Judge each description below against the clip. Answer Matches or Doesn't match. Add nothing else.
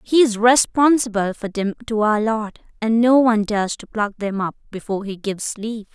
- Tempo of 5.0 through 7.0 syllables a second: Matches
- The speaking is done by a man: Doesn't match